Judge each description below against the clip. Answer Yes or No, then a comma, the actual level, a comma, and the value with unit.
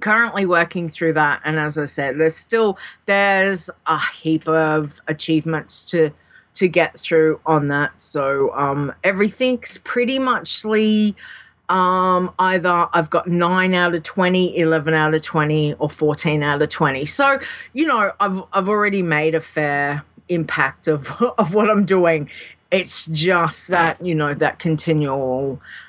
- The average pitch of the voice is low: No, medium, 170 Hz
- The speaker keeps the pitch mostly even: No, average, 3.8 semitones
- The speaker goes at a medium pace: Yes, average, 155 wpm